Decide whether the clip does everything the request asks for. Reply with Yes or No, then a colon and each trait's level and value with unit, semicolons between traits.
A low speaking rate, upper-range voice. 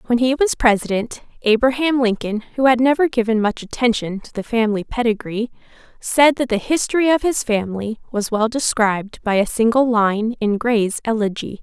No: average, 170 wpm; high, 230 Hz